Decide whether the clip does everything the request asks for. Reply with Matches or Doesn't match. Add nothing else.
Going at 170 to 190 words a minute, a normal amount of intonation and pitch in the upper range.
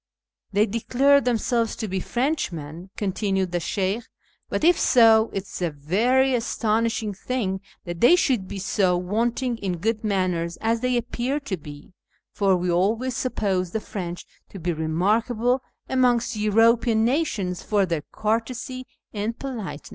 Doesn't match